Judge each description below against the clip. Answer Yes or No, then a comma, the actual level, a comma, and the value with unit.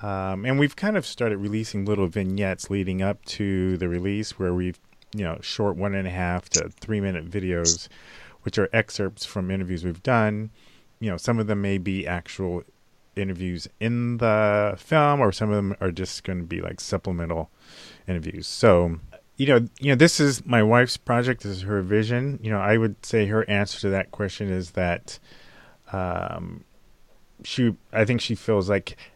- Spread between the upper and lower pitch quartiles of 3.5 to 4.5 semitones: No, average, 3.1 semitones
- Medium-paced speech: Yes, average, 185 wpm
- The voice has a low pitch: Yes, low, 100 Hz